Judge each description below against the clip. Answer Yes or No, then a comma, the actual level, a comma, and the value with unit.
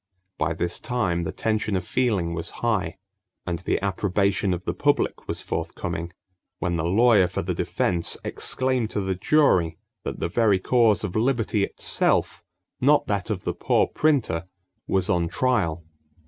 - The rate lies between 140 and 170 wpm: Yes, average, 160 wpm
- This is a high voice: No, very low, 95 Hz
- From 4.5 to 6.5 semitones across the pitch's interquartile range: Yes, average, 4.8 semitones